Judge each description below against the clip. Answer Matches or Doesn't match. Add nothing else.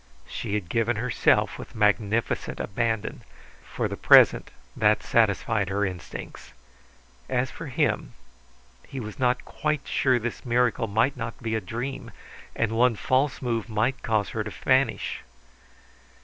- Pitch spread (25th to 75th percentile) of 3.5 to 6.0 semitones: Doesn't match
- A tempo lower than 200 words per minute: Matches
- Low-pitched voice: Matches